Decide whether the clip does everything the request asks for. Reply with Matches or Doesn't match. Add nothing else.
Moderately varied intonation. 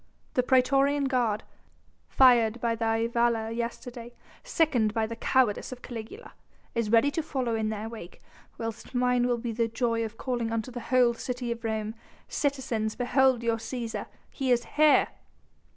Doesn't match